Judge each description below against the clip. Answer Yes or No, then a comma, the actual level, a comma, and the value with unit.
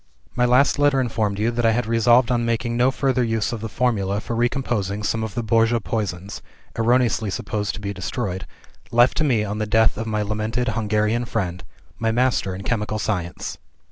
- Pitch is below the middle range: Yes, low, 115 Hz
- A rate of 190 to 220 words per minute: Yes, average, 195 wpm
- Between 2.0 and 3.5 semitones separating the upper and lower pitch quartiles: Yes, narrow, 2.4 semitones